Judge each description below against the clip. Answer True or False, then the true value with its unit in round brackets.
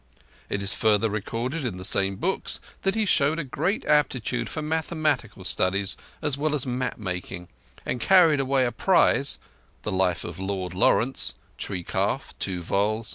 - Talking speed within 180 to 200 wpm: False (165 wpm)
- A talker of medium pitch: False (120 Hz)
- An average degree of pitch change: False (7.4 semitones)